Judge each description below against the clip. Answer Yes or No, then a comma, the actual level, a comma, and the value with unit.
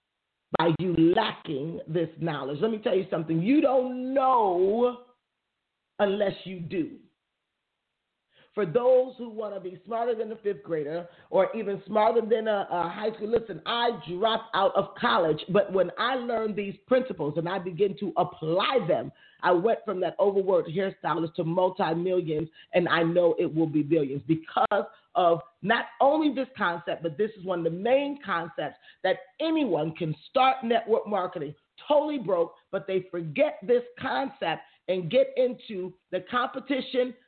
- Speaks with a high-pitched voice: Yes, high, 200 Hz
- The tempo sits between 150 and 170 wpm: Yes, average, 165 wpm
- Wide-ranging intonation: Yes, wide, 5.9 semitones